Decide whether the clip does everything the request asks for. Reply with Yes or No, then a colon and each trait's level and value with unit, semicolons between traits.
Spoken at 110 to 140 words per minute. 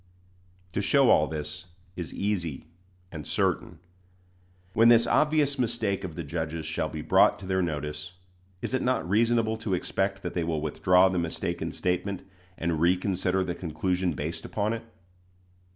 No: average, 155 wpm